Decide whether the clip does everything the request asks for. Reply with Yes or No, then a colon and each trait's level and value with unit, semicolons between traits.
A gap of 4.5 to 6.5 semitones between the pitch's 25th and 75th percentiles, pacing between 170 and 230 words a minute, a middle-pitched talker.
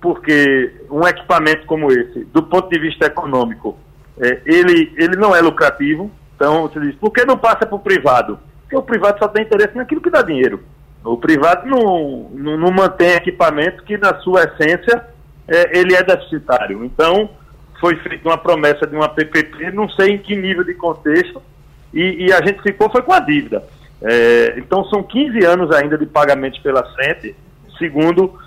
Yes: wide, 5.4 semitones; average, 180 wpm; medium, 175 Hz